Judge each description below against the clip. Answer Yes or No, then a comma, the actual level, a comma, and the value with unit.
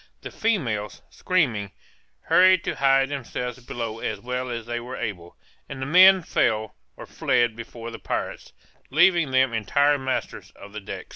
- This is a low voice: Yes, low, 125 Hz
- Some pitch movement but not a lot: Yes, average, 4.0 semitones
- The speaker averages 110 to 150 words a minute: No, average, 160 wpm